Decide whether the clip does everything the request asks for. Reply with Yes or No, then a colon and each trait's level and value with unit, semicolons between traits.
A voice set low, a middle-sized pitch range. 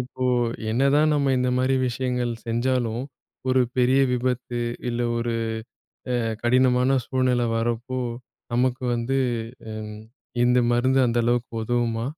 No: low, 125 Hz; narrow, 1.5 semitones